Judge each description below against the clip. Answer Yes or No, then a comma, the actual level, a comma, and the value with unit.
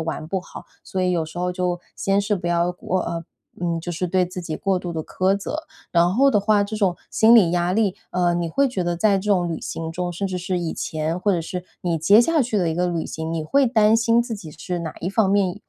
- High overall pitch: No, medium, 180 Hz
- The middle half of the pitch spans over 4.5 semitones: No, average, 2.9 semitones